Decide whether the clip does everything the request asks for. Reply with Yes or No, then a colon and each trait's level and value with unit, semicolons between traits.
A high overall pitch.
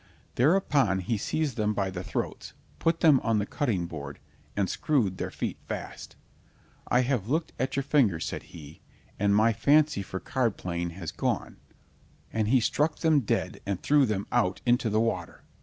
No: low, 110 Hz